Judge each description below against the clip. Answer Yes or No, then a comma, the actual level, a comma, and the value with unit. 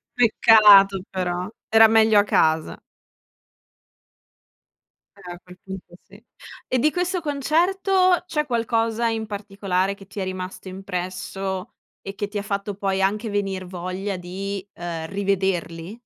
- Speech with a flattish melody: No, average, 3.1 semitones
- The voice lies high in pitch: Yes, high, 200 Hz